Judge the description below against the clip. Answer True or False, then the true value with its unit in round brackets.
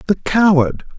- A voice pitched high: False (180 Hz)